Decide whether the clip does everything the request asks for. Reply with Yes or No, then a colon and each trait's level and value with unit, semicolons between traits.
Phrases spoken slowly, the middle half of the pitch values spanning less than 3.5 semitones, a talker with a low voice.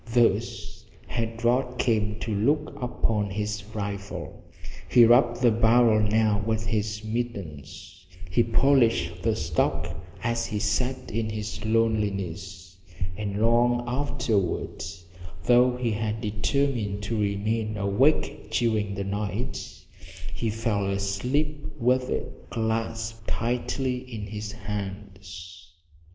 Yes: slow, 115 wpm; average, 2.7 semitones; low, 110 Hz